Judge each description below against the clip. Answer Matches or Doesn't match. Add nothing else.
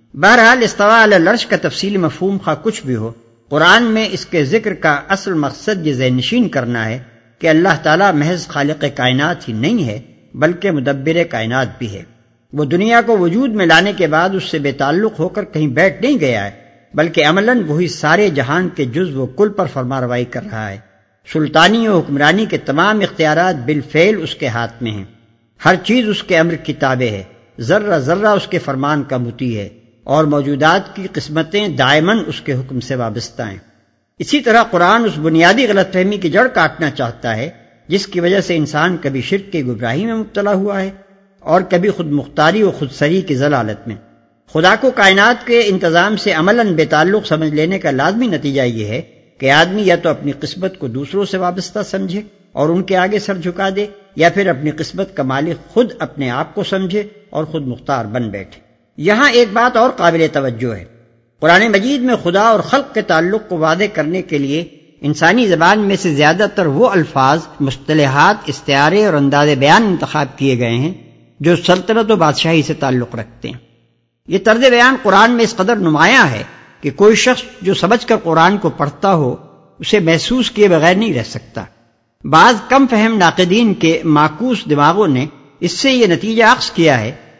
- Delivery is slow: Doesn't match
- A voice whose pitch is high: Doesn't match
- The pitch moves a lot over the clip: Matches